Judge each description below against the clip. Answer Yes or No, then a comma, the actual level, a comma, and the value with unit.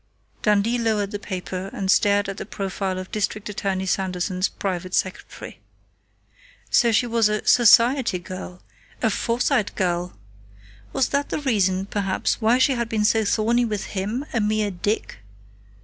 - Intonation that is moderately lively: Yes, average, 3.2 semitones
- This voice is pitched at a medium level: No, high, 205 Hz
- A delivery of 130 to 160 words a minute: Yes, average, 150 wpm